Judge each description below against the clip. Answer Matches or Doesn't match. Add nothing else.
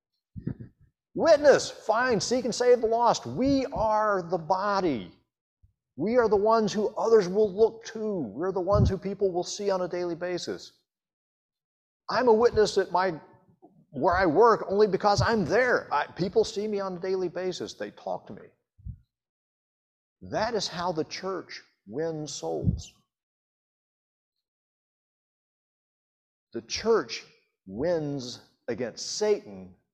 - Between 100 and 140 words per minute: Matches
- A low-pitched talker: Doesn't match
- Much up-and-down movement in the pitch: Doesn't match